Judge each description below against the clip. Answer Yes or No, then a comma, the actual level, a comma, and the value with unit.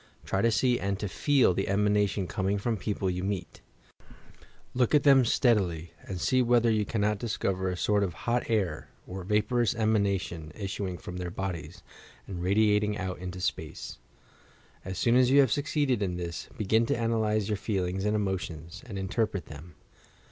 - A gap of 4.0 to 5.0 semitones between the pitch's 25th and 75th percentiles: No, average, 3.5 semitones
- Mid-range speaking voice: No, low, 100 Hz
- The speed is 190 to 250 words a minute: No, average, 175 wpm